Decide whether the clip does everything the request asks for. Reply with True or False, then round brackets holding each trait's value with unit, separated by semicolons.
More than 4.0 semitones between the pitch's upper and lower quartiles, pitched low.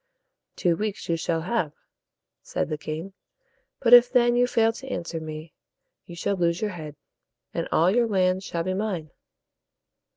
False (5.2 semitones; 185 Hz)